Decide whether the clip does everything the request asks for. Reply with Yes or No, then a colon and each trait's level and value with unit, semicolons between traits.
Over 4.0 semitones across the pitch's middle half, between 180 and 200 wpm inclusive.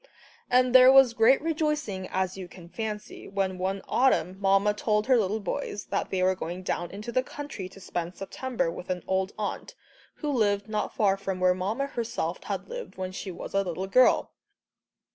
Yes: average, 4.8 semitones; average, 190 wpm